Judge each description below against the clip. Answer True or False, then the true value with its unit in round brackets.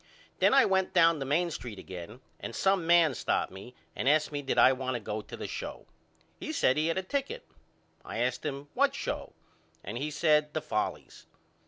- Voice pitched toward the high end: False (150 Hz)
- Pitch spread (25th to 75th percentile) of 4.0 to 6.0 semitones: True (5.1 semitones)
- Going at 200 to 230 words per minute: True (205 wpm)